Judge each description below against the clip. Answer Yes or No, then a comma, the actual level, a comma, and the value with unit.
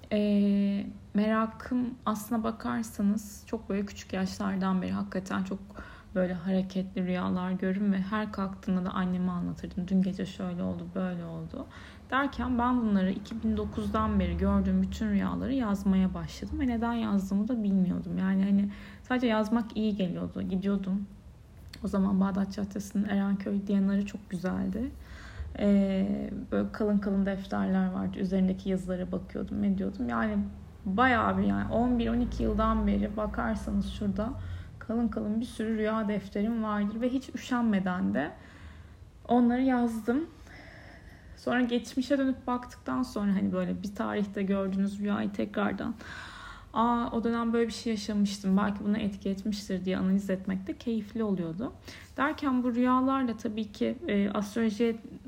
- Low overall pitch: No, high, 205 Hz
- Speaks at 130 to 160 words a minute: Yes, average, 135 wpm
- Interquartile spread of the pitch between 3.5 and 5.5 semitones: No, average, 3.0 semitones